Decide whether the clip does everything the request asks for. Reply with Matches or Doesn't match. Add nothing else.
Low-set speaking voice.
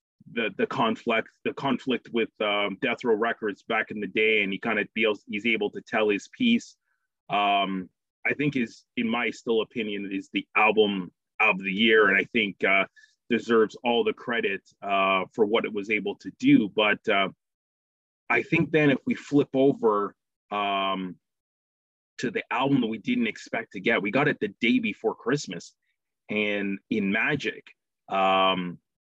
Matches